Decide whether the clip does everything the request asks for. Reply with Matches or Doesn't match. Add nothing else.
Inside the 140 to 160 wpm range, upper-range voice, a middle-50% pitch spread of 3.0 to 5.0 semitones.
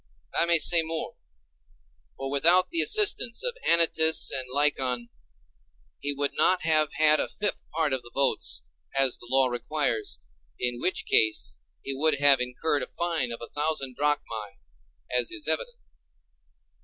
Doesn't match